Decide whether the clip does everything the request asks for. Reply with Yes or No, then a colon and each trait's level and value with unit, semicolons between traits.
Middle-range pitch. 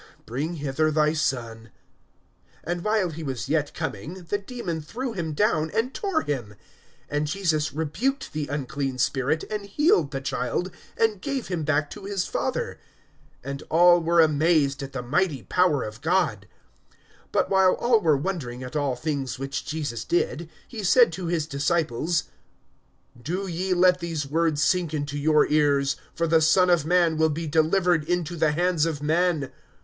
Yes: medium, 160 Hz